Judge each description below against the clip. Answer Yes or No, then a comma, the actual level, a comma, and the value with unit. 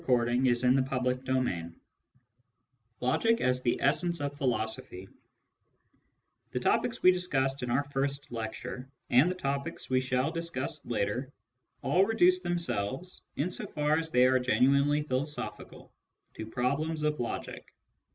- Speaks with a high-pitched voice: No, low, 135 Hz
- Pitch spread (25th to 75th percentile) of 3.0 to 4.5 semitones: Yes, average, 3.3 semitones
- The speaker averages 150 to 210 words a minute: No, average, 140 wpm